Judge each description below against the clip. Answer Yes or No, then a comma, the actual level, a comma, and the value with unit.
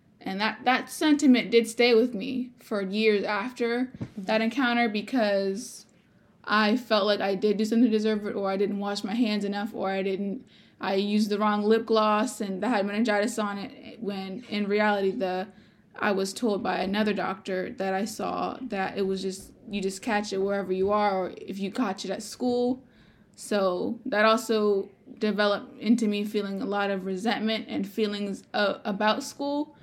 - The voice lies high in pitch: Yes, high, 210 Hz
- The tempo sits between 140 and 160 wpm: No, average, 185 wpm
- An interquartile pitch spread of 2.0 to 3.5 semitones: Yes, narrow, 2.6 semitones